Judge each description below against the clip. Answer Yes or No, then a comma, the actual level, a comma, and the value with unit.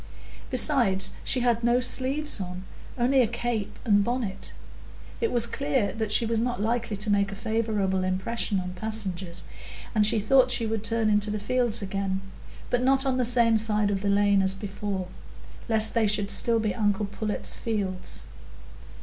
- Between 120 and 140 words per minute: No, average, 170 wpm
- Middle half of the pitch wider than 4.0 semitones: No, average, 3.1 semitones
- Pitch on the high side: Yes, high, 215 Hz